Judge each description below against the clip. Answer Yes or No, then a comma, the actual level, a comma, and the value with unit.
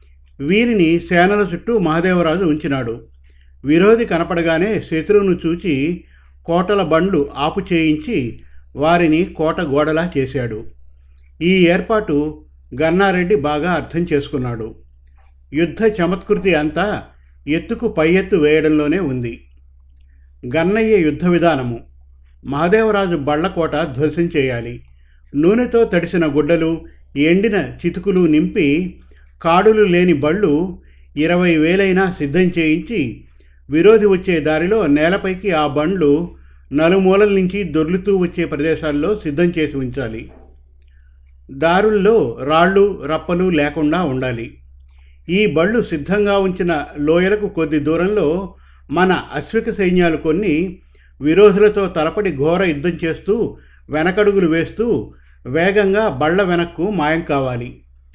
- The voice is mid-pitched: Yes, medium, 160 Hz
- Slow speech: No, average, 95 wpm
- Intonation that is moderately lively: No, wide, 6.0 semitones